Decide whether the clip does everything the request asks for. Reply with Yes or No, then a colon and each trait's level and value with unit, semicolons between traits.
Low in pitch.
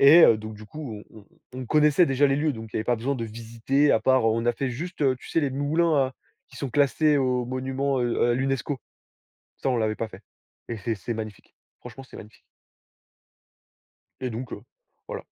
Yes: low, 130 Hz